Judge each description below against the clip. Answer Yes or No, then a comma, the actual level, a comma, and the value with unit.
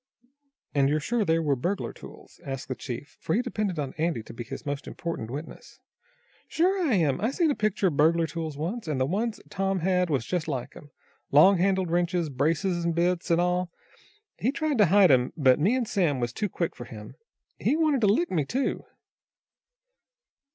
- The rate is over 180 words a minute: Yes, average, 200 wpm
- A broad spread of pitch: Yes, wide, 5.7 semitones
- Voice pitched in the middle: Yes, medium, 170 Hz